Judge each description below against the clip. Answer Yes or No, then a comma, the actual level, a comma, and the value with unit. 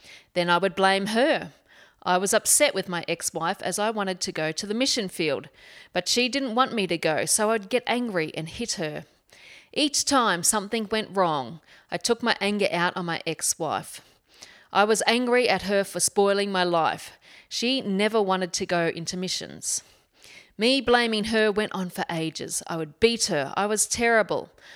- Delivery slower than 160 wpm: No, average, 190 wpm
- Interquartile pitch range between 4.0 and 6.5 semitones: Yes, average, 4.3 semitones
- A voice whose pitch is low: No, high, 200 Hz